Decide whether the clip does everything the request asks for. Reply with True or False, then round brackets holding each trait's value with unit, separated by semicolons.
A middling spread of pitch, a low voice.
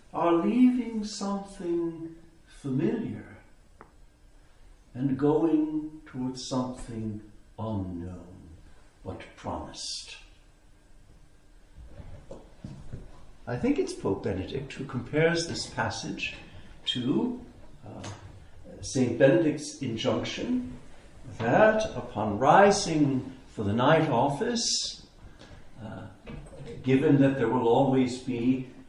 False (6.5 semitones; 130 Hz)